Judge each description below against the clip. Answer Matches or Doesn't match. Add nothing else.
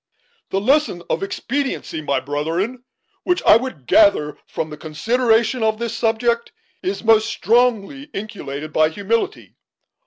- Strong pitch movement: Matches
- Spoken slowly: Matches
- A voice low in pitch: Doesn't match